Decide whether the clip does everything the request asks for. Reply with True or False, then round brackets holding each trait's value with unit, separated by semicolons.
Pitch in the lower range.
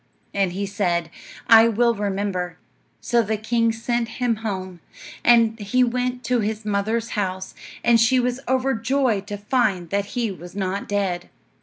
False (220 Hz)